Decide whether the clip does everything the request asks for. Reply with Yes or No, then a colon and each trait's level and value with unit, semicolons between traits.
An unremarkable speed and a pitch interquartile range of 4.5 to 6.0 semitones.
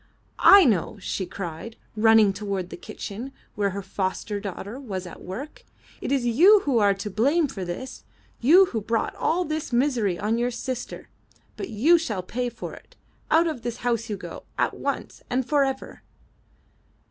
Yes: average, 175 wpm; average, 5.3 semitones